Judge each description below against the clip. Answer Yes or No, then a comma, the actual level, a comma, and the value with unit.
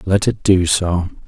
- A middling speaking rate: Yes, average, 190 wpm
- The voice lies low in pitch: Yes, very low, 90 Hz